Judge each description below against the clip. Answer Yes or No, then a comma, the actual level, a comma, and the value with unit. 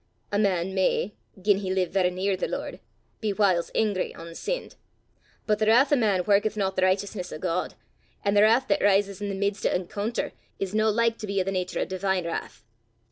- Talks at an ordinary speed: No, fast, 215 wpm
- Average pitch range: No, narrow, 2.2 semitones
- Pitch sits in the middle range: No, high, 200 Hz